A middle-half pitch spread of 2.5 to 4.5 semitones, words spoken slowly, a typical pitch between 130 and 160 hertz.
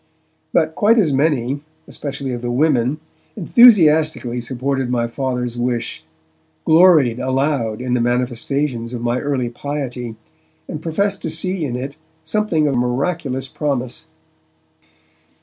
Yes: average, 4.1 semitones; slow, 125 wpm; low, 135 Hz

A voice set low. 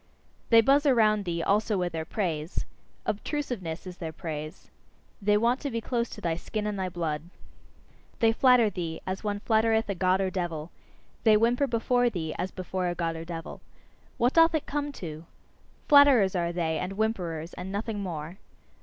No: high, 195 Hz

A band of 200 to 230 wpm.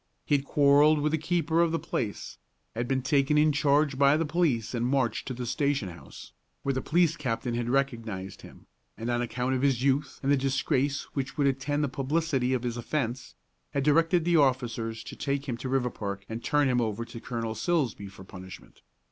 Yes: fast, 205 wpm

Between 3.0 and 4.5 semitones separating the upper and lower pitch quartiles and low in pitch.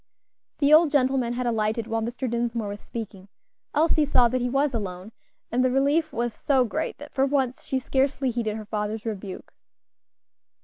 No: average, 3.6 semitones; high, 240 Hz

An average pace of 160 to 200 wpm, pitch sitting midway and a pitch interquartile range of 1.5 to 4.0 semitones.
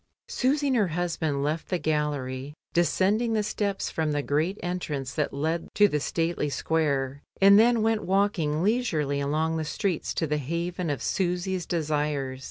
No: average, 170 wpm; medium, 165 Hz; average, 4.6 semitones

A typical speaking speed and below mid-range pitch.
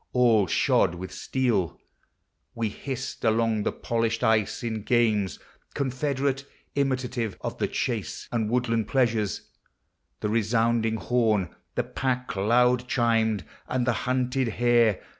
No: slow, 120 wpm; low, 115 Hz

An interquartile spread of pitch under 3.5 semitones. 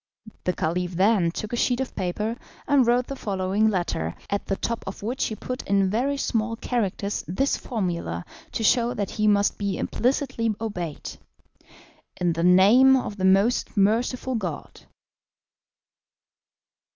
No: average, 4.3 semitones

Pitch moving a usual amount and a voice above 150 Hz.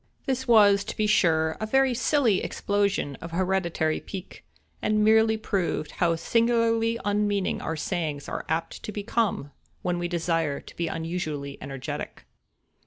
Yes: average, 5.0 semitones; high, 190 Hz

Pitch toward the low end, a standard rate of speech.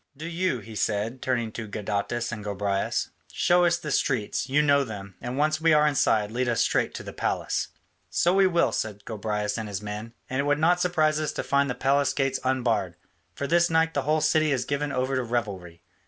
No: low, 130 Hz; fast, 215 wpm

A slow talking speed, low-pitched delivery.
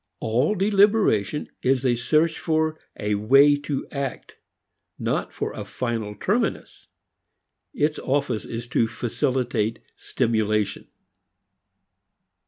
Yes: slow, 100 wpm; low, 130 Hz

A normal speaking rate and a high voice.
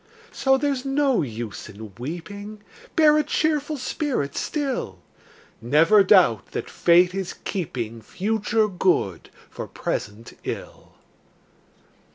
No: slow, 110 wpm; high, 195 Hz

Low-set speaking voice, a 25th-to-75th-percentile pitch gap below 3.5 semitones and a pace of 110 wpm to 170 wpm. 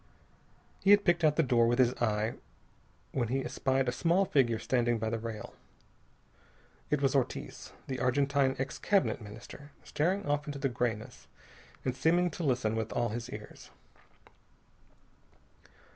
No: low, 130 Hz; average, 3.8 semitones; average, 150 wpm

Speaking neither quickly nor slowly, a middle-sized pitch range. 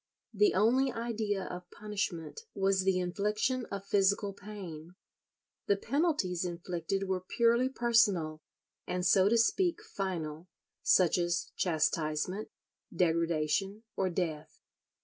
No: slow, 110 wpm; average, 3.7 semitones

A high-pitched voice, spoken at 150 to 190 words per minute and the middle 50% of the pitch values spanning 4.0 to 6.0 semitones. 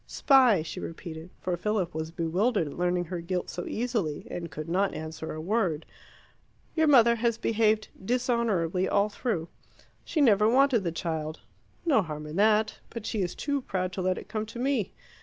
Yes: high, 195 Hz; average, 180 wpm; wide, 5.6 semitones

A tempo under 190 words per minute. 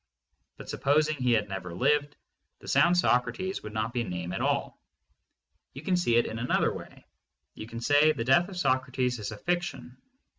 No: average, 195 wpm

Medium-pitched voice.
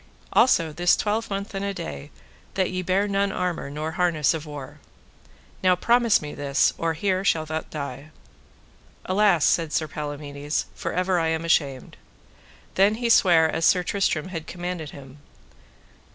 Yes: medium, 165 Hz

